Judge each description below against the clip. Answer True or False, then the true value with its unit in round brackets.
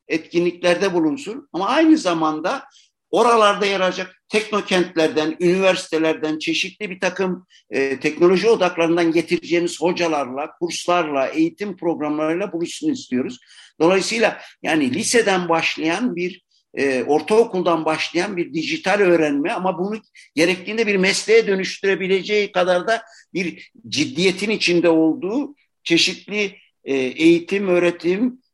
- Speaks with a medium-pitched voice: True (180 Hz)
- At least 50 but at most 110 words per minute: True (105 wpm)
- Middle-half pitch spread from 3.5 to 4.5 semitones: True (3.8 semitones)